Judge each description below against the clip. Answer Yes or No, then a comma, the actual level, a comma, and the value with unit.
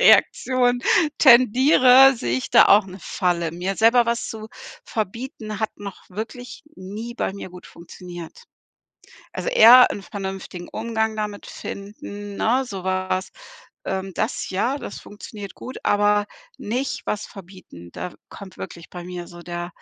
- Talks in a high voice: Yes, high, 205 Hz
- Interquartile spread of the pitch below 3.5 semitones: No, average, 4.0 semitones